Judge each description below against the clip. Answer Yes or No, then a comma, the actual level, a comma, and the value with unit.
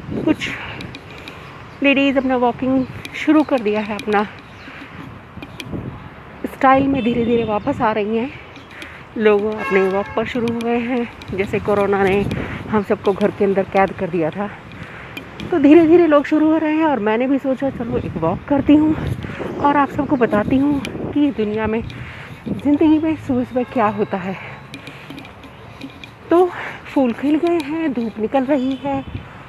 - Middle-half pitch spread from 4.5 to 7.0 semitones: Yes, wide, 5.4 semitones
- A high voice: Yes, high, 245 Hz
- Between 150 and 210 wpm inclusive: Yes, average, 160 wpm